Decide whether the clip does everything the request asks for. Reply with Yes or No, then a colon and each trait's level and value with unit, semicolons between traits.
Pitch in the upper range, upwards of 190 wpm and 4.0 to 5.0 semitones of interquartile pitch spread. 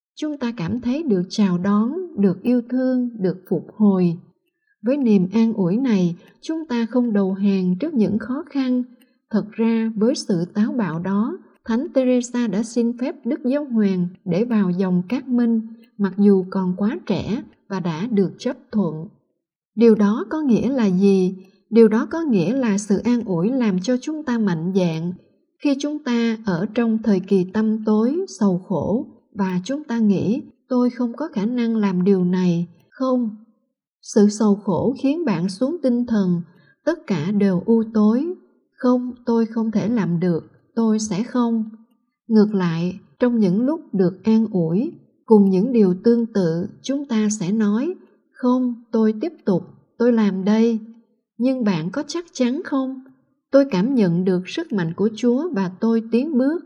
No: high, 225 Hz; average, 175 wpm; average, 4.3 semitones